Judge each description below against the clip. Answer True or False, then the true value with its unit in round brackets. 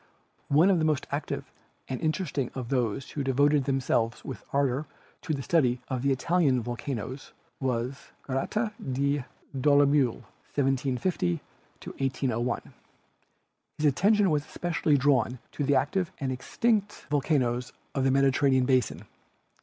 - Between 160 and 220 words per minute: False (140 wpm)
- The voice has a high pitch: False (135 Hz)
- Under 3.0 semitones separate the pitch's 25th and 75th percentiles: True (2.6 semitones)